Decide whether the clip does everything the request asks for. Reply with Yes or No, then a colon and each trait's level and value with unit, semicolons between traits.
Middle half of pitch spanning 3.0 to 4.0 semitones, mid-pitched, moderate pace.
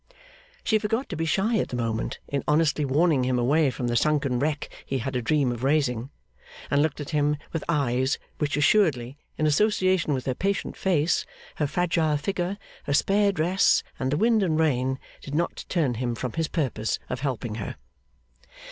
No: average, 4.6 semitones; medium, 150 Hz; average, 185 wpm